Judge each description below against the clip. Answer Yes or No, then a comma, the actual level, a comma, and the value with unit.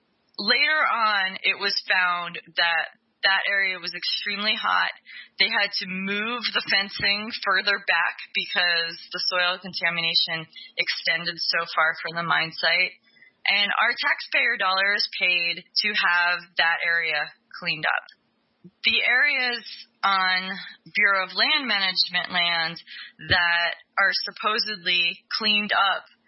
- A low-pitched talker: No, medium, 185 Hz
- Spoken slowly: Yes, slow, 125 wpm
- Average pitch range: Yes, average, 3.0 semitones